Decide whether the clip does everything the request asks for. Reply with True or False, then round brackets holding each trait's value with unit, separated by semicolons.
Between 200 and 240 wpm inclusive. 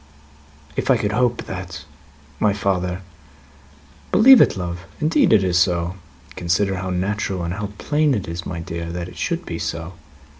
False (175 wpm)